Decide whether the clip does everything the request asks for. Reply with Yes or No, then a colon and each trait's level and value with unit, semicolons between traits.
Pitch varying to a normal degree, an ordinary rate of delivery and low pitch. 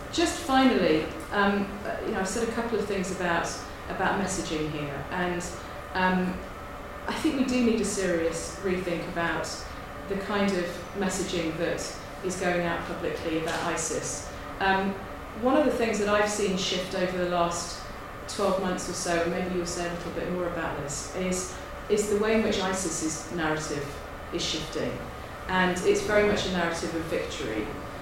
No: average, 3.0 semitones; average, 175 wpm; medium, 185 Hz